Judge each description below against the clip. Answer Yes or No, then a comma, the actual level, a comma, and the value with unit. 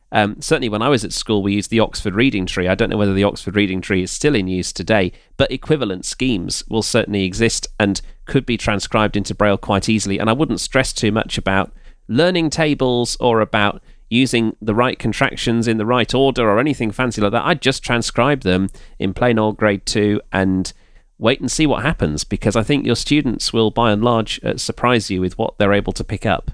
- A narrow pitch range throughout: No, average, 3.5 semitones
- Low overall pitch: Yes, low, 110 Hz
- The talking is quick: Yes, fast, 220 wpm